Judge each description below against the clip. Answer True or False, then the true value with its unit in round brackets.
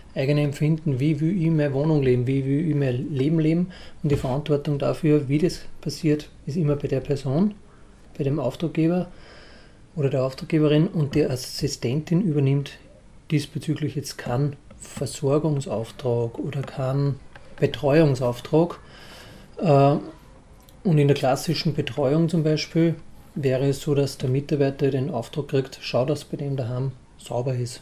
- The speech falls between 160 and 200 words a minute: False (140 wpm)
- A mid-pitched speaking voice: True (145 Hz)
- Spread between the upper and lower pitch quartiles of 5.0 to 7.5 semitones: False (2.4 semitones)